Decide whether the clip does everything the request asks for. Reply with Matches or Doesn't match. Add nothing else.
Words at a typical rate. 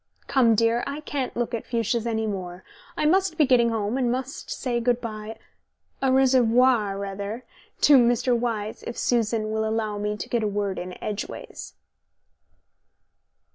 Matches